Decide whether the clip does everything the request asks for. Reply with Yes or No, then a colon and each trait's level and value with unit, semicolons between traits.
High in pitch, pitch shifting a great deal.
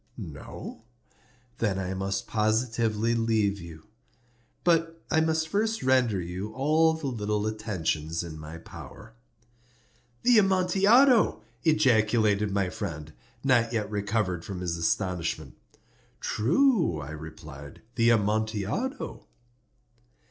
No: low, 110 Hz; wide, 8.4 semitones